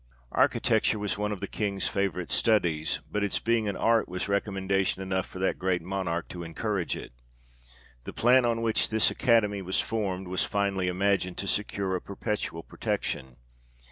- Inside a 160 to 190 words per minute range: Yes, average, 170 wpm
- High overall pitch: No, low, 100 Hz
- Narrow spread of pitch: Yes, narrow, 2.3 semitones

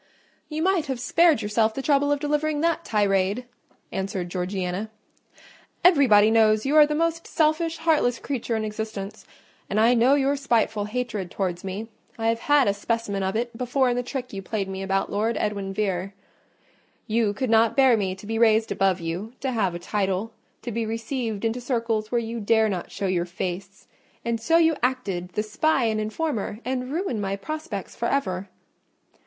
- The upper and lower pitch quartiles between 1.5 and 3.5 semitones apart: No, average, 4.9 semitones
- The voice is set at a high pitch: Yes, high, 225 Hz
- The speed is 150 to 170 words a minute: No, average, 185 wpm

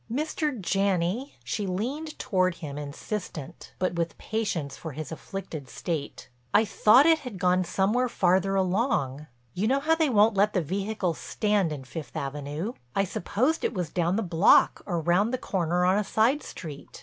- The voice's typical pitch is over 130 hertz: Yes, high, 190 Hz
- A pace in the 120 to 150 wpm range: No, average, 175 wpm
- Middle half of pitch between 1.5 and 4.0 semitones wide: No, average, 4.7 semitones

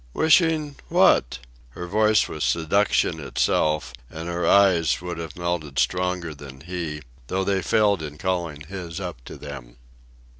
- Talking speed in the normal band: Yes, average, 145 wpm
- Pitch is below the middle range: Yes, very low, 85 Hz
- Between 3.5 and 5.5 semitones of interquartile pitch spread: Yes, average, 4.0 semitones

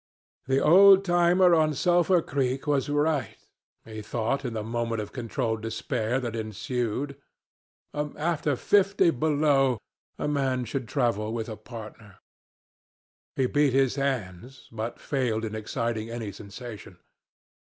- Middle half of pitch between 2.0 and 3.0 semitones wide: No, average, 4.7 semitones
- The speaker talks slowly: Yes, slow, 130 wpm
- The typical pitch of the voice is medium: No, low, 130 Hz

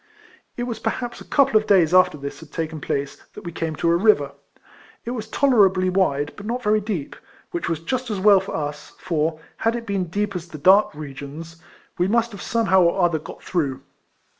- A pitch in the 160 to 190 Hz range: Yes, medium, 185 Hz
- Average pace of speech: No, fast, 215 wpm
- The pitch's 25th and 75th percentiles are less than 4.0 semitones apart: No, average, 5.1 semitones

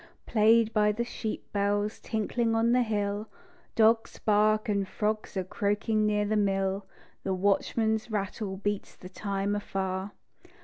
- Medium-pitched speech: No, high, 210 Hz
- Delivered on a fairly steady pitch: Yes, narrow, 1.6 semitones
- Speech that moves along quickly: No, average, 140 wpm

